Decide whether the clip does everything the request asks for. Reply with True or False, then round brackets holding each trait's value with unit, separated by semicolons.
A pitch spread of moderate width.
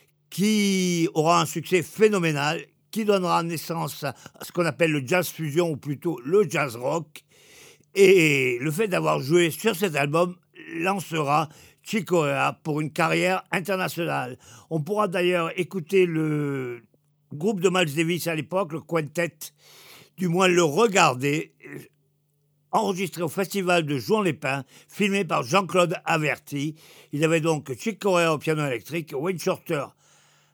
True (3.9 semitones)